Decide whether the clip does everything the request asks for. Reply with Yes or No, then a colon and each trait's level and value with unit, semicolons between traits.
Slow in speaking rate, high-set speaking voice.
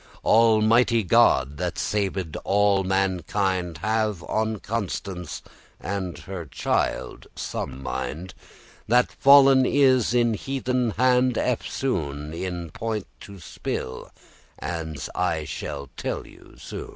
No: slow, 115 wpm; low, 100 Hz